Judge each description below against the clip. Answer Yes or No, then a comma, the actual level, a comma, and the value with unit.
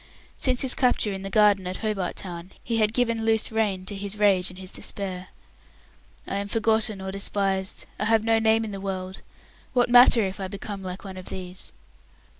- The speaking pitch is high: Yes, high, 200 Hz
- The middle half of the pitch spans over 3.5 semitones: No, average, 2.7 semitones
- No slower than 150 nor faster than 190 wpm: No, average, 200 wpm